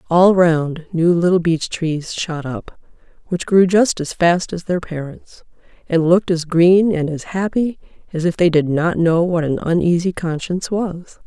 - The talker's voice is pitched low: No, medium, 170 Hz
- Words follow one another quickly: No, average, 180 wpm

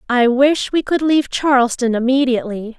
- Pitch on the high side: Yes, very high, 260 Hz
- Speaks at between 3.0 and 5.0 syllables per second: No, 5.4 syllables/s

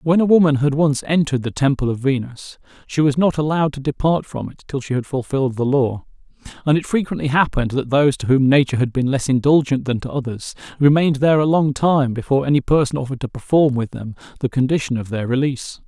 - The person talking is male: Yes, male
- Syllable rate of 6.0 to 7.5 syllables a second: Yes, 6.4 syllables/s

